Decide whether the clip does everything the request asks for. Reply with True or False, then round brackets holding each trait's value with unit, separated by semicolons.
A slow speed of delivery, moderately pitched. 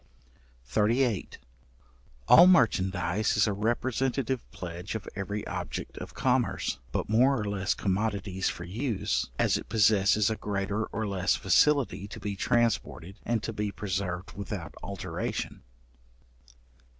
False (125 wpm; 105 Hz)